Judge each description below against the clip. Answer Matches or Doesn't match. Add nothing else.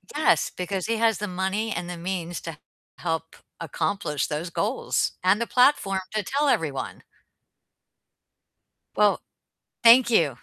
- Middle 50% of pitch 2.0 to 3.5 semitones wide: Doesn't match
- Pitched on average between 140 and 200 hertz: Matches